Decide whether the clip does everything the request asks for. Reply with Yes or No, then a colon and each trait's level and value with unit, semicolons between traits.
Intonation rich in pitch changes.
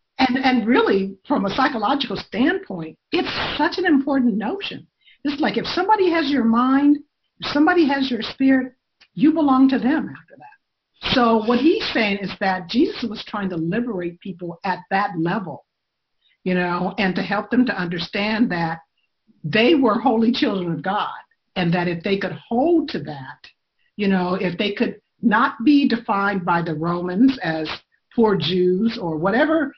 Yes: wide, 6.7 semitones